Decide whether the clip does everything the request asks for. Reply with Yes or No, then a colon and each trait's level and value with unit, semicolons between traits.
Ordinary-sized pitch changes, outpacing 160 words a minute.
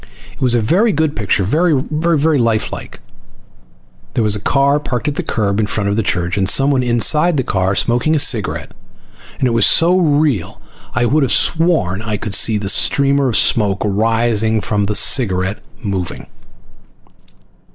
No: wide, 5.9 semitones; average, 170 wpm